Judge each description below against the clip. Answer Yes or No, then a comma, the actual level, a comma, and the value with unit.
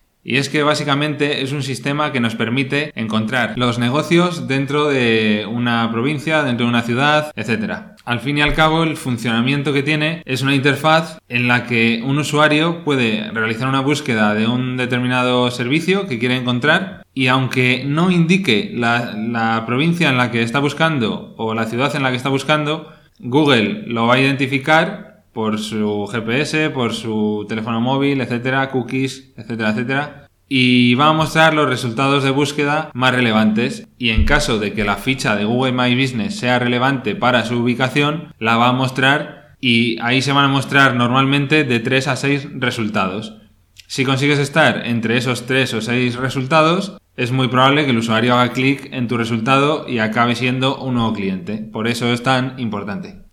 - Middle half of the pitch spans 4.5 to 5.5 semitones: No, average, 3.7 semitones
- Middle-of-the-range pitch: No, low, 130 Hz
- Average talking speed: Yes, average, 180 wpm